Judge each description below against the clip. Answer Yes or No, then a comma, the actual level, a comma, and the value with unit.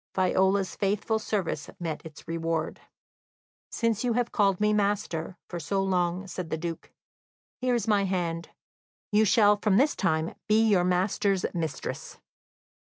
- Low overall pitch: No, high, 190 Hz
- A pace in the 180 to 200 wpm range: No, average, 145 wpm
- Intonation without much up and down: No, average, 3.6 semitones